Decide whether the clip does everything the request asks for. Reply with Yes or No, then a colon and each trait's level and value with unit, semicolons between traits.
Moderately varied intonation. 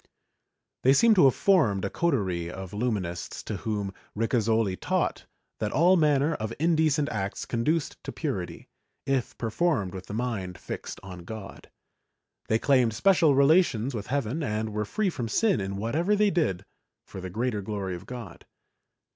No: wide, 6.9 semitones